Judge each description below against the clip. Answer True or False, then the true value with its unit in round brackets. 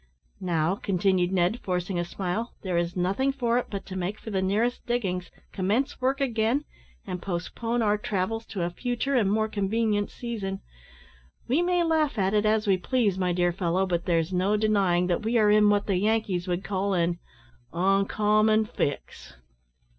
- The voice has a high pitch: True (200 Hz)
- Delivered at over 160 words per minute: True (175 wpm)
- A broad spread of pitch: False (3.7 semitones)